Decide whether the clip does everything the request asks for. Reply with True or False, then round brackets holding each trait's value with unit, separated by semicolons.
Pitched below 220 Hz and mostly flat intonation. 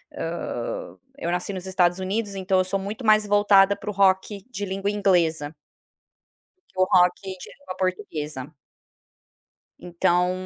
True (190 Hz; 2.2 semitones)